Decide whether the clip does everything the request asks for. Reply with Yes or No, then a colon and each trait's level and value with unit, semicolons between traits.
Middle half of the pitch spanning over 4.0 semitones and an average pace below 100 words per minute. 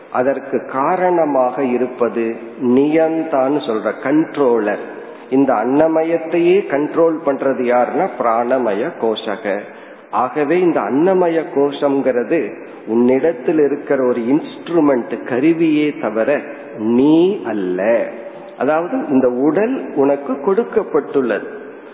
Yes: average, 4.8 semitones; average, 80 wpm